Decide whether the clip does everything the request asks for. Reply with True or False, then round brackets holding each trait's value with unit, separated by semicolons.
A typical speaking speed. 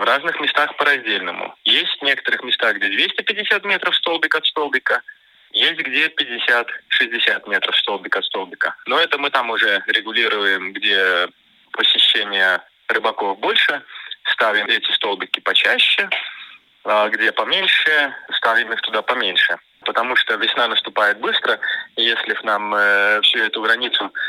True (135 wpm)